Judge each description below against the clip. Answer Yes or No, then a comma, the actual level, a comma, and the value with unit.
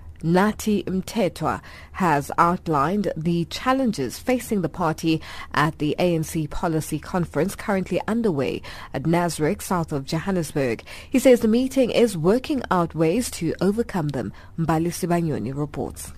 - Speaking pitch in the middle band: Yes, medium, 170 Hz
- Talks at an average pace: No, slow, 130 wpm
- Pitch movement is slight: No, average, 4.3 semitones